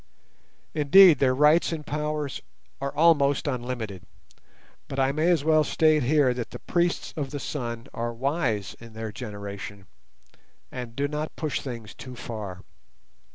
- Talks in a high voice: No, low, 135 Hz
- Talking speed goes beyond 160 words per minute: No, average, 150 wpm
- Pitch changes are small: No, average, 4.7 semitones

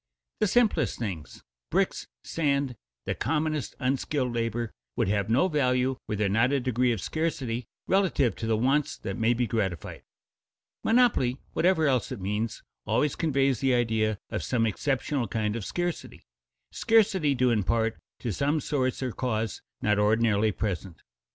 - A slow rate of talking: No, average, 155 wpm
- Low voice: Yes, low, 125 Hz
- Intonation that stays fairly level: No, average, 4.5 semitones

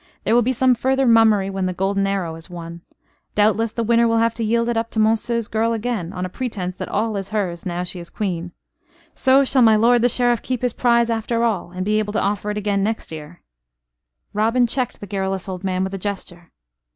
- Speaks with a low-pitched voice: No, high, 210 Hz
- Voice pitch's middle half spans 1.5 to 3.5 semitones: No, average, 3.9 semitones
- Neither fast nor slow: No, fast, 235 wpm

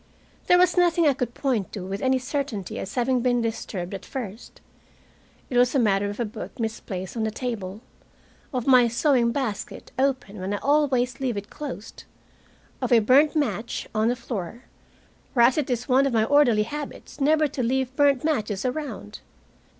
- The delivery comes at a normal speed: Yes, average, 180 wpm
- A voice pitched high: Yes, high, 245 Hz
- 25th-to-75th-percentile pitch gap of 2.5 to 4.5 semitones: Yes, average, 4.1 semitones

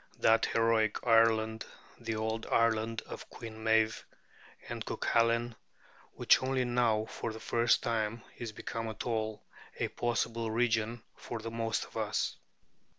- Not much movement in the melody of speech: Yes, narrow, 0.9 semitones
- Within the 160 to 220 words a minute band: No, average, 140 wpm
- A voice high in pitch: No, low, 115 Hz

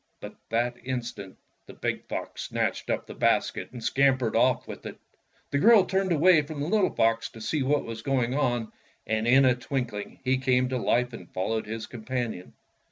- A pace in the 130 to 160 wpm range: No, average, 195 wpm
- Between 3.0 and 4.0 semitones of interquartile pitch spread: Yes, average, 3.3 semitones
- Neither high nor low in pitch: No, low, 125 Hz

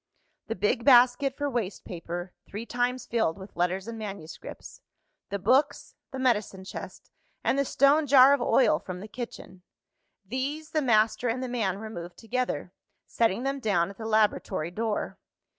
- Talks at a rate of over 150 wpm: Yes, average, 160 wpm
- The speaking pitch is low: No, high, 225 Hz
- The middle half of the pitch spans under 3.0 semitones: No, average, 4.9 semitones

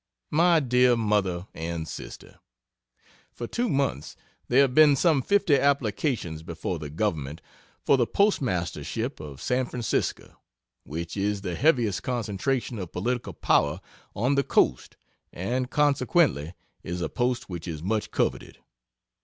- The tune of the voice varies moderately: No, wide, 7.7 semitones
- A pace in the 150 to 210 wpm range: No, slow, 135 wpm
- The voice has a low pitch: Yes, low, 115 Hz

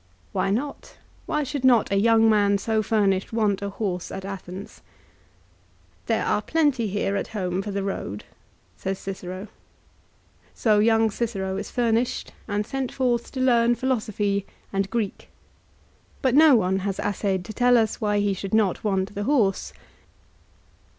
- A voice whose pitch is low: No, high, 210 Hz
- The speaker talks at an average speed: Yes, average, 155 wpm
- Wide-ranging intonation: No, average, 3.2 semitones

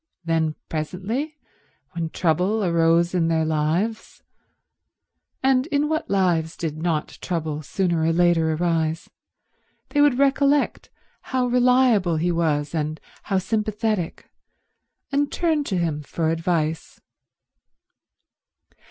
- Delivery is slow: Yes, slow, 105 wpm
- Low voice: No, medium, 175 Hz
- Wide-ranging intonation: Yes, wide, 6.1 semitones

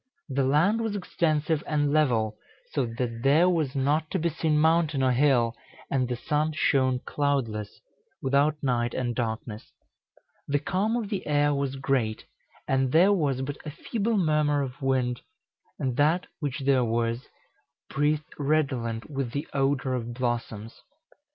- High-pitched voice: No, medium, 140 Hz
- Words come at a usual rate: Yes, average, 150 wpm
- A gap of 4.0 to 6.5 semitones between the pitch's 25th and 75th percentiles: No, average, 3.6 semitones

